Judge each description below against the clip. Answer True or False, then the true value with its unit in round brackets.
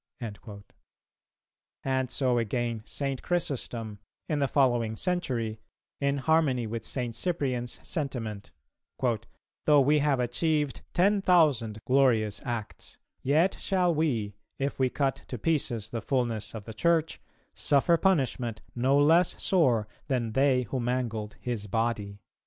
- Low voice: True (130 Hz)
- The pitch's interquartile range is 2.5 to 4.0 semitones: False (4.4 semitones)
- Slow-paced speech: True (130 wpm)